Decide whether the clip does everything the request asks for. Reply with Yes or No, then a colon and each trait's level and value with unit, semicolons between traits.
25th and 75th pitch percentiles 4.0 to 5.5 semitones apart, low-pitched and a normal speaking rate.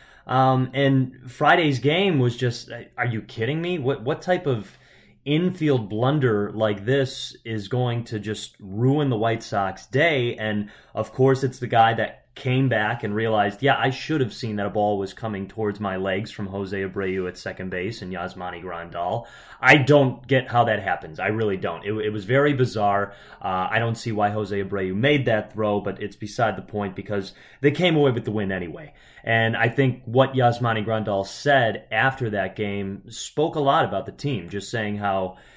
Yes: average, 4.7 semitones; low, 115 Hz; average, 195 wpm